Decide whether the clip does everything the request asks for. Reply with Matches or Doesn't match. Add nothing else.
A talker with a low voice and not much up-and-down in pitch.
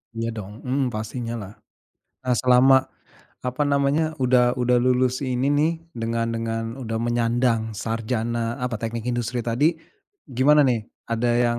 Matches